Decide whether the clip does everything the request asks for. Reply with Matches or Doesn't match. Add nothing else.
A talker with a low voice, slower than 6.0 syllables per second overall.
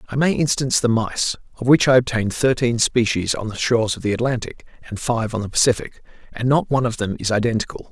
Doesn't match